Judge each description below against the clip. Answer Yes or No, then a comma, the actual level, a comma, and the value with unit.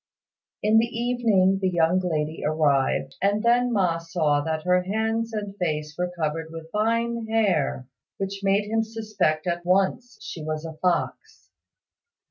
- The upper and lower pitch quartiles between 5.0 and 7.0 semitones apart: Yes, wide, 5.4 semitones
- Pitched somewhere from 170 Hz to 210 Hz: Yes, medium, 185 Hz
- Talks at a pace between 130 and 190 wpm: Yes, average, 150 wpm